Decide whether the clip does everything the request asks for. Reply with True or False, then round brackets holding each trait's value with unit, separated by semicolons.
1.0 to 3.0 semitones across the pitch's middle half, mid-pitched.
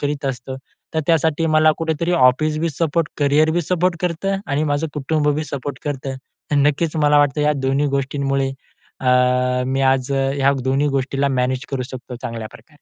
True (2.5 semitones; 145 Hz)